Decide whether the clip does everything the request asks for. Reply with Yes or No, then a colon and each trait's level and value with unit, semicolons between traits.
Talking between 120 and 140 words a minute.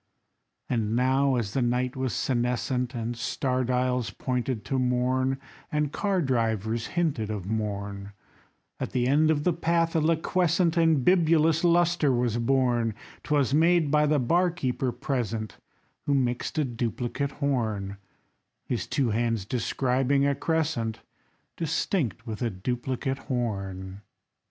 Yes: slow, 135 wpm